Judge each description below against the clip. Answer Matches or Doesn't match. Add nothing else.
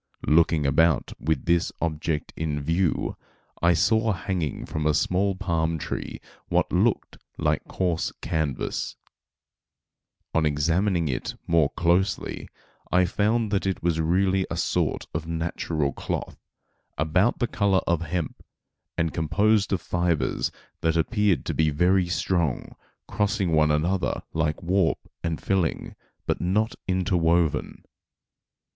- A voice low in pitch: Matches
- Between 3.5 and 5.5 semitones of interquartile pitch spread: Doesn't match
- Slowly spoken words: Matches